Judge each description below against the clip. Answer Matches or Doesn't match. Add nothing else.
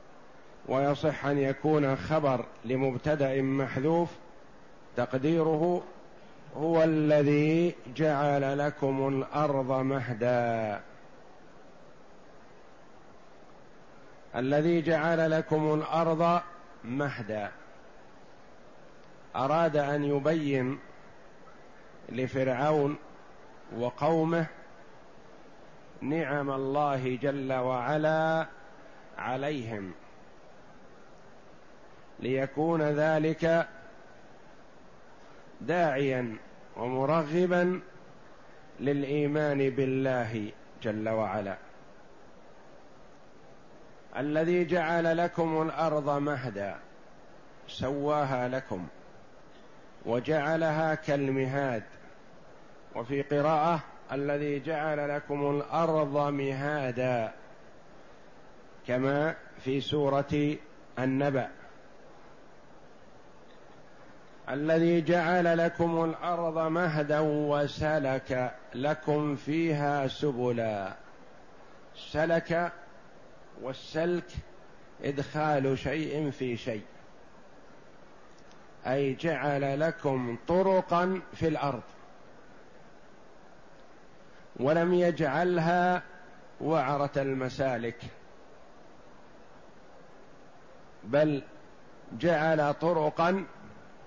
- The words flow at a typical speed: Doesn't match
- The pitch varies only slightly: Doesn't match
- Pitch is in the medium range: Matches